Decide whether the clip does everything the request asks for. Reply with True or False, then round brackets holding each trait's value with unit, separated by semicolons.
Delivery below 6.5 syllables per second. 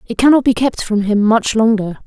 True (5.3 syllables/s)